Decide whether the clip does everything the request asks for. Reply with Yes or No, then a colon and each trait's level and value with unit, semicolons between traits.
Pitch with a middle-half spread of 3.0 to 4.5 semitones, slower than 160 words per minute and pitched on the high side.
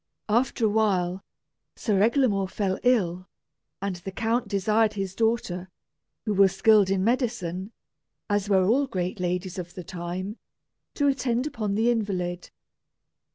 Yes: average, 3.5 semitones; average, 140 wpm; high, 200 Hz